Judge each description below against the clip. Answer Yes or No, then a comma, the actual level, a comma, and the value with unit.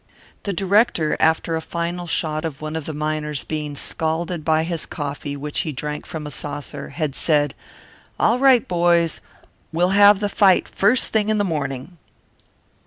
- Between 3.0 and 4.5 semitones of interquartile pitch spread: Yes, average, 3.3 semitones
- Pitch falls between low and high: Yes, medium, 160 Hz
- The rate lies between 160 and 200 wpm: Yes, average, 170 wpm